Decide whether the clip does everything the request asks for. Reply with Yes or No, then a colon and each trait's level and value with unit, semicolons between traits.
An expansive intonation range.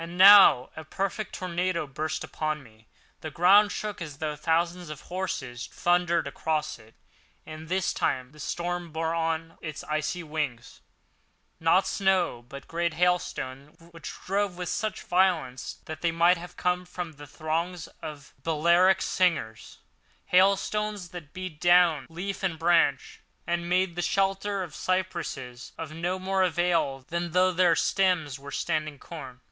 No: average, 2.9 semitones